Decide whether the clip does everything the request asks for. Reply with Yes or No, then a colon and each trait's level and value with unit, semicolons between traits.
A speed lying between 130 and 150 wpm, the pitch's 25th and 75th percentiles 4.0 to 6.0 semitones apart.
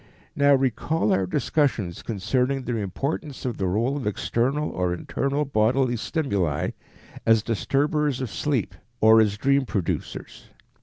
Yes: average, 140 wpm; average, 5.0 semitones